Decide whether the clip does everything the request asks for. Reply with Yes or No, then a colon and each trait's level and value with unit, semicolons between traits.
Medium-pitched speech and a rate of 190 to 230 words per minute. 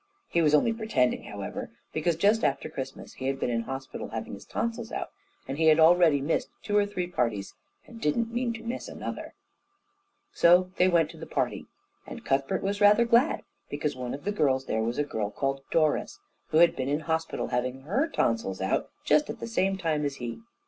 Yes: medium, 160 Hz; fast, 205 wpm